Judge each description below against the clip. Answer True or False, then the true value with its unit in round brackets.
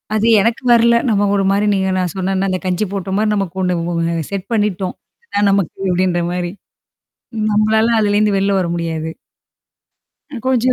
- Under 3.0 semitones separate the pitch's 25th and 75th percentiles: True (2.4 semitones)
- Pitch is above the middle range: True (195 Hz)